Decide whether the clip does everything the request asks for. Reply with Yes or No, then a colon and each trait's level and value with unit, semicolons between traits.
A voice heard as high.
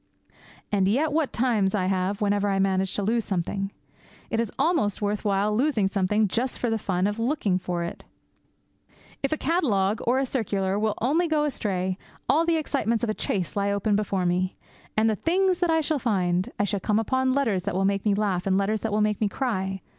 Yes: high, 210 Hz